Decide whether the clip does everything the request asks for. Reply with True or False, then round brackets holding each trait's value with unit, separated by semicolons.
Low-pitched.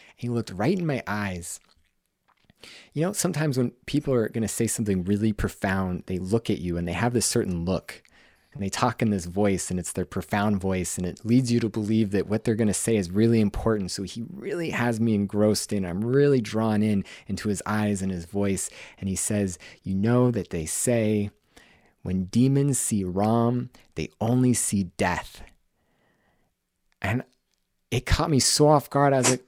True (105 Hz)